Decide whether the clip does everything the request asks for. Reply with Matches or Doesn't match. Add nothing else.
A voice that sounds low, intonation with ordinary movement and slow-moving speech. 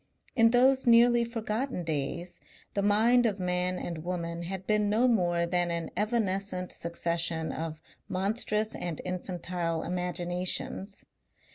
Doesn't match